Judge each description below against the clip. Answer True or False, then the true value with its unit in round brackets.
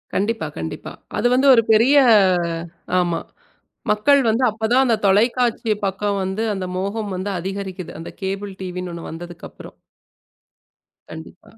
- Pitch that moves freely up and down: False (3.6 semitones)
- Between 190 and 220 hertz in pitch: True (200 Hz)